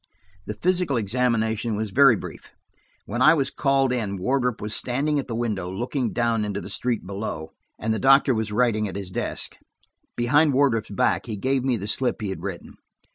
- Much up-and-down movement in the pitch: No, average, 3.9 semitones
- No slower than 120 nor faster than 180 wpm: No, average, 190 wpm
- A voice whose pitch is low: Yes, low, 115 Hz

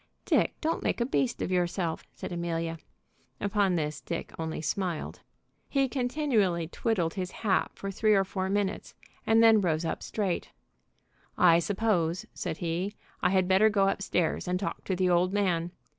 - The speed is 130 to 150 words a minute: No, average, 170 wpm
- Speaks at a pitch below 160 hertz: No, medium, 185 Hz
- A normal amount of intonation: Yes, average, 3.3 semitones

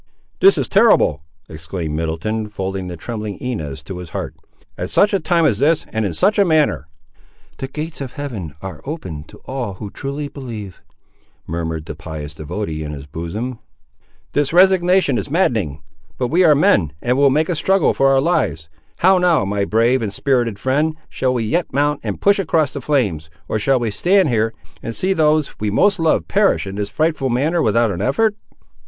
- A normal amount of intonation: No, wide, 8.4 semitones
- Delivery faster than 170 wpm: Yes, average, 190 wpm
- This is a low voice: Yes, low, 125 Hz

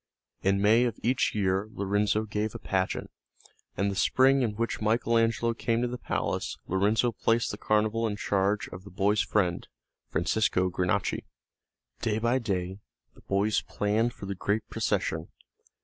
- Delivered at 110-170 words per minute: Yes, average, 160 wpm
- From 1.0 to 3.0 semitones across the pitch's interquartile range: Yes, narrow, 2.6 semitones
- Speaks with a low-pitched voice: Yes, low, 105 Hz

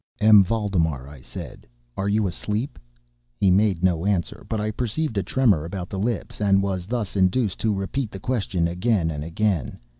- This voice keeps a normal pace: Yes, average, 180 wpm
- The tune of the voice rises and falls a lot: No, average, 3.4 semitones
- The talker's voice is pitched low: Yes, low, 100 Hz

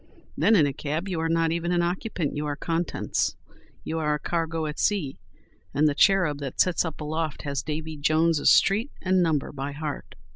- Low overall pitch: No, medium, 160 Hz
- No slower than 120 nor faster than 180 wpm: No, average, 195 wpm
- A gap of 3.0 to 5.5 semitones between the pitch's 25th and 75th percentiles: No, narrow, 2.6 semitones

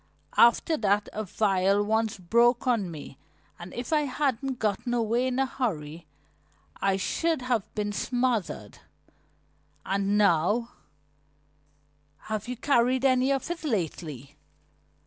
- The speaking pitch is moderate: No, high, 215 Hz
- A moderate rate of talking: No, slow, 125 wpm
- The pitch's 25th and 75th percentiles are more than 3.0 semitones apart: Yes, wide, 5.5 semitones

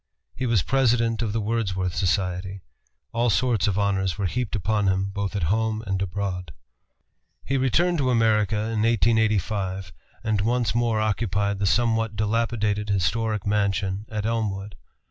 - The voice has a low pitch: Yes, low, 105 Hz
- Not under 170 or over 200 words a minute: No, average, 145 wpm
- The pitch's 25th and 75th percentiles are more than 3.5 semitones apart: No, average, 2.7 semitones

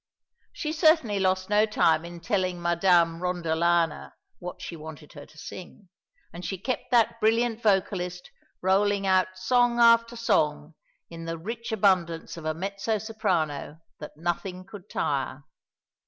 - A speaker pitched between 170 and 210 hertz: Yes, medium, 185 Hz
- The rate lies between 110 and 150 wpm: Yes, average, 140 wpm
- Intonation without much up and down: No, average, 4.2 semitones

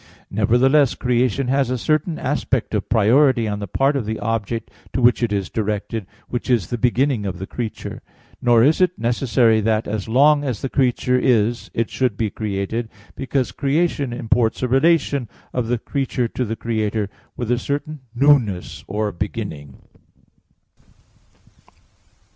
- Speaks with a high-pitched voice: No, low, 120 Hz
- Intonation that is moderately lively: Yes, average, 3.5 semitones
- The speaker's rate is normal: Yes, average, 155 wpm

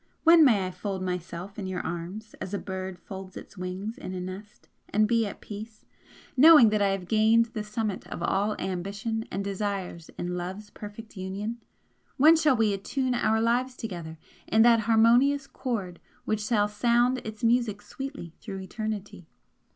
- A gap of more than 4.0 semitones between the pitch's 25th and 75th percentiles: No, average, 3.5 semitones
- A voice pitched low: No, high, 210 Hz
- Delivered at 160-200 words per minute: Yes, average, 170 wpm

